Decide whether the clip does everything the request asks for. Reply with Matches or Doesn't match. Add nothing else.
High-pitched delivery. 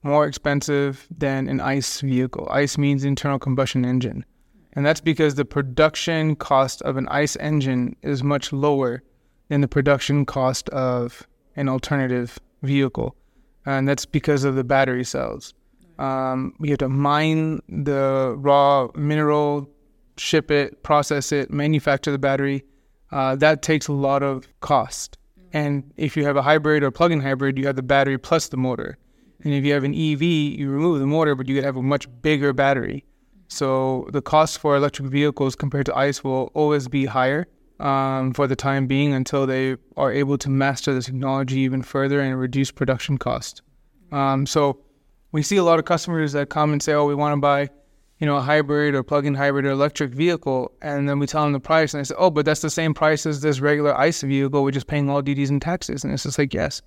Doesn't match